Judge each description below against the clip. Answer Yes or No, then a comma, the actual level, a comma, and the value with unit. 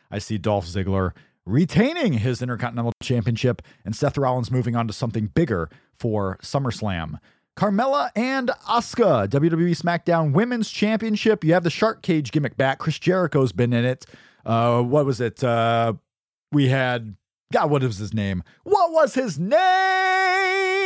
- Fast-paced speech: No, average, 150 wpm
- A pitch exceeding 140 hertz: No, low, 135 Hz